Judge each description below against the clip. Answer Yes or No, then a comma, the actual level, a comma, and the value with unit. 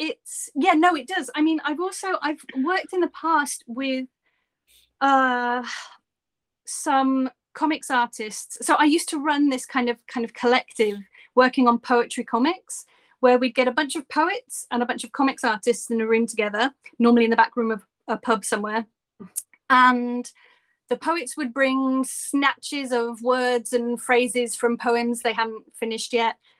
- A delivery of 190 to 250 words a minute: No, average, 170 wpm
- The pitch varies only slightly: No, average, 4.0 semitones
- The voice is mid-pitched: No, very high, 255 Hz